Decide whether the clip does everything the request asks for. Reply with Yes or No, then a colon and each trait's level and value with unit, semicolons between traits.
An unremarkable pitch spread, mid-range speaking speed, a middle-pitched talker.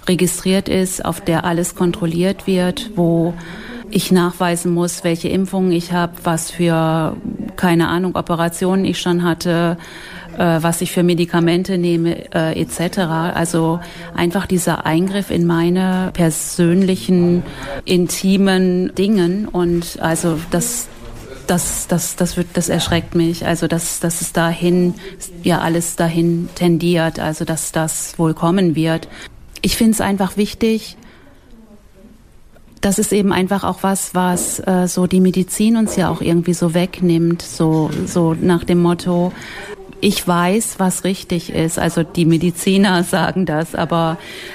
No: narrow, 1.8 semitones; average, 140 wpm; medium, 175 Hz